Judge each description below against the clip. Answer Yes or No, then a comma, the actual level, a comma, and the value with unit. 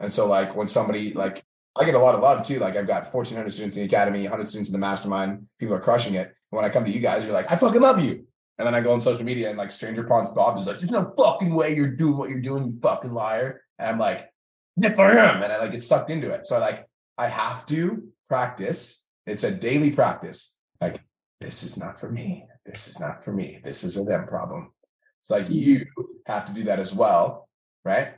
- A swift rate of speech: Yes, fast, 250 wpm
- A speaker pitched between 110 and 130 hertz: Yes, low, 120 Hz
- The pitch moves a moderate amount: No, wide, 6.1 semitones